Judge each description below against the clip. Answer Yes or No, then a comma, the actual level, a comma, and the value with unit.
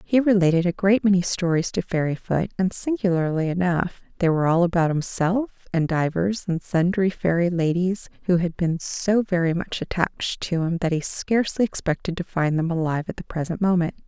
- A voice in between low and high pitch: Yes, medium, 175 Hz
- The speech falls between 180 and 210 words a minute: Yes, average, 185 wpm